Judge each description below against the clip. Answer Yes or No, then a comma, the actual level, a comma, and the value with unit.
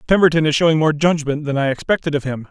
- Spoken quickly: Yes, fast, 240 wpm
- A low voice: No, medium, 155 Hz